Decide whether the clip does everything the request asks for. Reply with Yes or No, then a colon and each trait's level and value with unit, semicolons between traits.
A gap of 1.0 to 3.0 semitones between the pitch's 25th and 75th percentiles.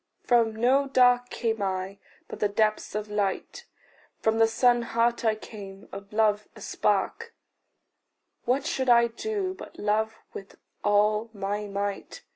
Yes: average, 2.7 semitones